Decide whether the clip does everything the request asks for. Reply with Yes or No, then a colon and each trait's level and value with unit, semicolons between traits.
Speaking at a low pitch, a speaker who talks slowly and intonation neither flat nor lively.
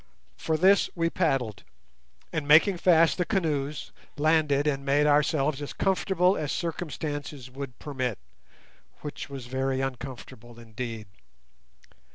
No: medium, 145 Hz; slow, 120 wpm; average, 3.5 semitones